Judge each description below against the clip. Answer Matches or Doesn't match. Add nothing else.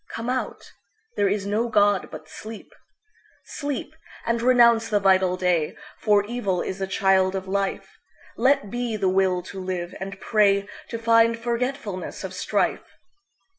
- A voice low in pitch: Doesn't match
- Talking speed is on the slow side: Matches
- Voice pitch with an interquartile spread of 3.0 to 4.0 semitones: Matches